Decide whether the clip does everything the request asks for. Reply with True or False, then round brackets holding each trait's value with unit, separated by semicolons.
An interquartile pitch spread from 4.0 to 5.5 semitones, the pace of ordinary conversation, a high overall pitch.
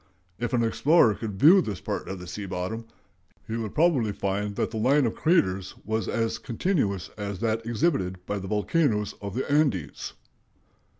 False (4.6 semitones; 175 wpm; 110 Hz)